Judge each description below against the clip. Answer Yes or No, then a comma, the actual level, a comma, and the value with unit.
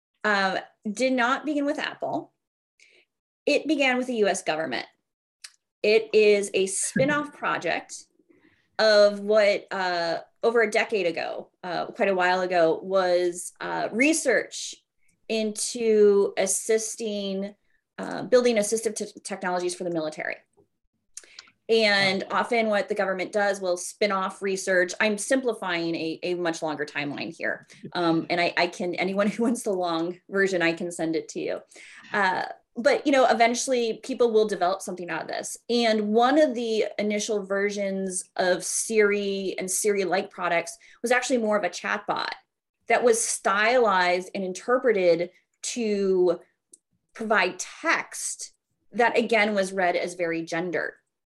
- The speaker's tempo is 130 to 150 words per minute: Yes, average, 145 wpm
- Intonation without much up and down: No, average, 3.9 semitones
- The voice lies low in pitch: No, high, 200 Hz